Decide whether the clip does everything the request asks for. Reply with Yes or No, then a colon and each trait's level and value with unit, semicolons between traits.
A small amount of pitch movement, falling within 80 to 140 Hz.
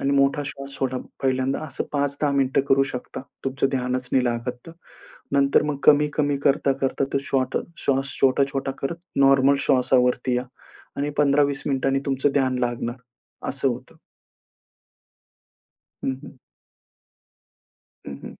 Yes: narrow, 1.4 semitones; low, 135 Hz